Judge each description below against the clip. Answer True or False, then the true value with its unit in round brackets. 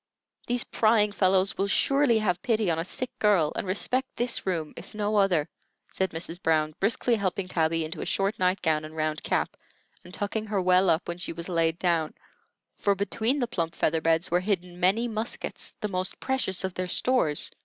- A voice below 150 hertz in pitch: False (185 Hz)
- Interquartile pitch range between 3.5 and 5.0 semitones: True (4.2 semitones)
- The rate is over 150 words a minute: True (195 wpm)